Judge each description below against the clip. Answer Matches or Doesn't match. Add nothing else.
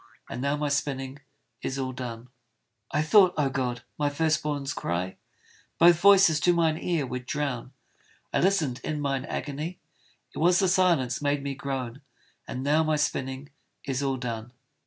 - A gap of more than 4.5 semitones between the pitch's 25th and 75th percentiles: Doesn't match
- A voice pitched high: Doesn't match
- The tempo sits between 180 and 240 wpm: Doesn't match